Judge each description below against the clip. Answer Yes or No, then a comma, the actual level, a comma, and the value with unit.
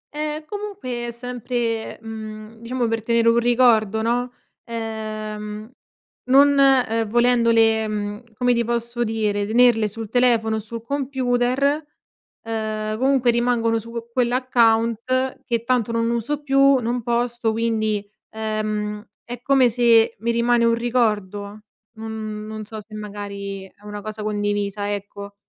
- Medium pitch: No, high, 230 Hz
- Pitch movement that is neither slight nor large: No, narrow, 2.2 semitones